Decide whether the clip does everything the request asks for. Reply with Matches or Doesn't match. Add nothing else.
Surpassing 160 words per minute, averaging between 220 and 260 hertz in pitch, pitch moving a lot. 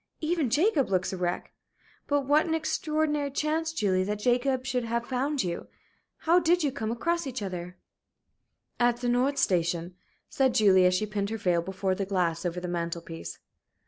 Matches